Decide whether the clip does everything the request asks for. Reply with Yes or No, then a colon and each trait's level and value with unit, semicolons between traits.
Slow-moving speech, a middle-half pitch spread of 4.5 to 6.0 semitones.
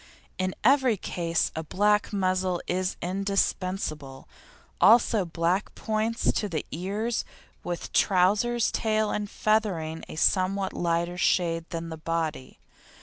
No: slow, 120 wpm; average, 3.8 semitones